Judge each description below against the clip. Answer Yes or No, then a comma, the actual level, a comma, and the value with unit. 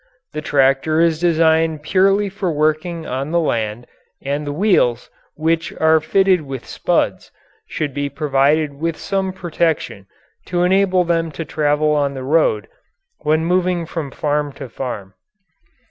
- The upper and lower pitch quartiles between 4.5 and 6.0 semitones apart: No, average, 3.2 semitones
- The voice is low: No, medium, 155 Hz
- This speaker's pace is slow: No, average, 145 wpm